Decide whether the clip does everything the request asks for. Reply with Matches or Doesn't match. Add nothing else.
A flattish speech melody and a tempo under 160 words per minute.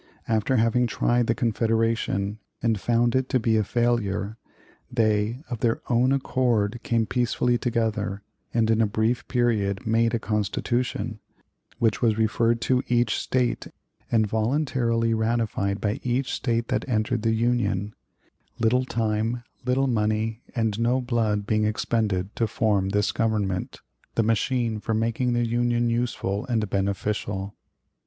Matches